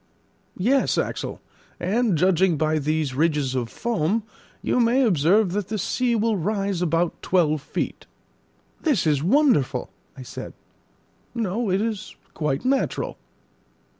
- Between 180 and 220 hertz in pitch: Yes, medium, 185 Hz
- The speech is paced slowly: Yes, slow, 130 wpm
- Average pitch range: No, wide, 6.5 semitones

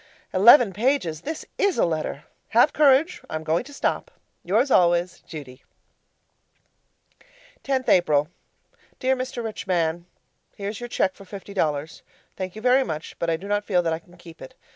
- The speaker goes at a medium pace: Yes, average, 165 wpm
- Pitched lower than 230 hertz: Yes, high, 190 Hz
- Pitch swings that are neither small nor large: No, wide, 7.0 semitones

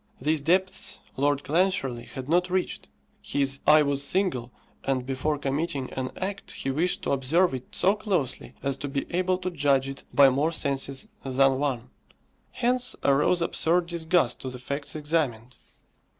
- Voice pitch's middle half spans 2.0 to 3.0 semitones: No, average, 4.6 semitones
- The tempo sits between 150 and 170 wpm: Yes, average, 160 wpm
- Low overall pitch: No, medium, 145 Hz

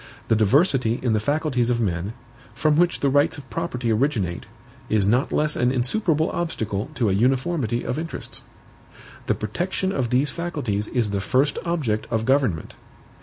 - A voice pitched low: Yes, low, 125 Hz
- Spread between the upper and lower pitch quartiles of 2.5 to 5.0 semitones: No, wide, 5.6 semitones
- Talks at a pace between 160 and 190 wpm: Yes, average, 165 wpm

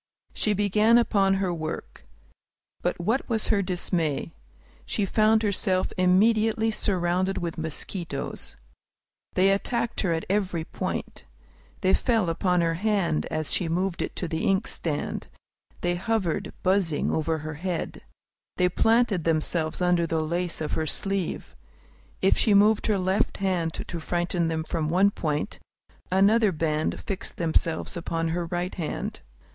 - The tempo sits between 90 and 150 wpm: Yes, average, 145 wpm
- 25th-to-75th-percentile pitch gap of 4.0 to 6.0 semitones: No, average, 3.4 semitones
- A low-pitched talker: No, medium, 180 Hz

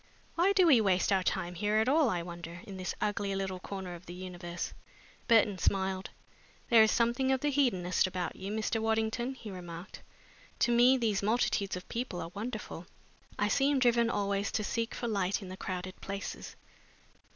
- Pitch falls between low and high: No, high, 205 Hz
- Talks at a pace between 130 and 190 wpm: Yes, average, 185 wpm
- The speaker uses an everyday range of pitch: Yes, average, 4.1 semitones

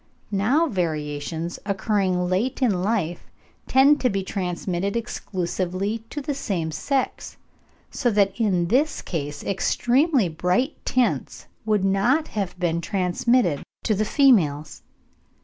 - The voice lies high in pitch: Yes, high, 195 Hz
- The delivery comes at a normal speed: No, slow, 120 wpm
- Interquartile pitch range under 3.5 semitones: No, wide, 5.5 semitones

